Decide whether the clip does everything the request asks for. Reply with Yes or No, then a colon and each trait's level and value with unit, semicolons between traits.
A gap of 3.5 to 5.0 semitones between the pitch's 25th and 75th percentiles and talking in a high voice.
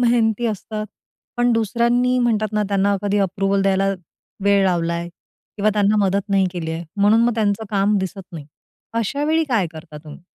No: average, 2.8 semitones; high, 205 Hz